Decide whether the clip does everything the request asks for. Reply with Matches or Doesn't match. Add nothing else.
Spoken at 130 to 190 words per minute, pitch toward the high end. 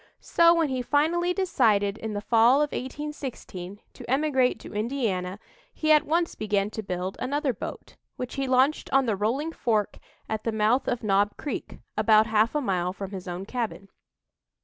Matches